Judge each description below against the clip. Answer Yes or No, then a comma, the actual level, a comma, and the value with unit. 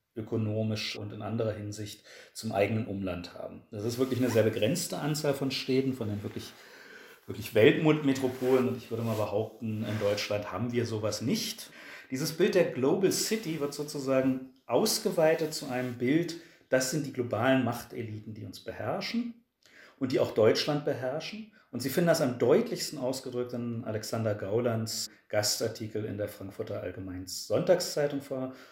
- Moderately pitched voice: No, low, 125 Hz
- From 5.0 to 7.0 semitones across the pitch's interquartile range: Yes, average, 5.3 semitones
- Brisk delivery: No, average, 155 wpm